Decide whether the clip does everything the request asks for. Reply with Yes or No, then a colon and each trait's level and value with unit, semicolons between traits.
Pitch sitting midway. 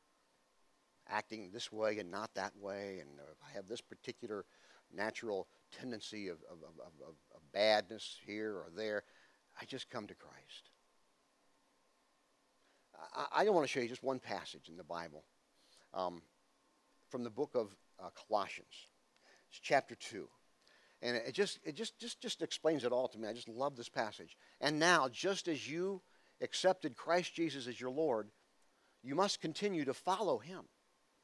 No: low, 125 Hz